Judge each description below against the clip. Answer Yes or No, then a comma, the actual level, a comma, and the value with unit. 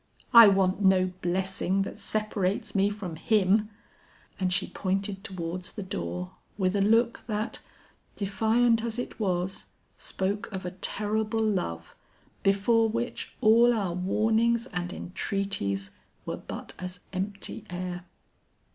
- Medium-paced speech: No, slow, 130 wpm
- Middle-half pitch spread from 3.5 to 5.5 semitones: No, average, 3.0 semitones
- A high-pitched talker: Yes, high, 195 Hz